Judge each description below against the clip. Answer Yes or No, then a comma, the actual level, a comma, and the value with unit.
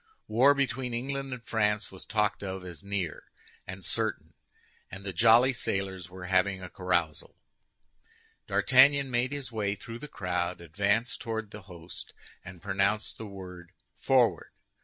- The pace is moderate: Yes, average, 145 wpm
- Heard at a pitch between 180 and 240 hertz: No, low, 100 Hz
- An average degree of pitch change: Yes, average, 4.3 semitones